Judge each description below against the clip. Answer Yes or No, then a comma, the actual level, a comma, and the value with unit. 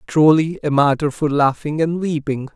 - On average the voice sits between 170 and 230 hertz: No, medium, 150 Hz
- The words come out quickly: No, average, 165 wpm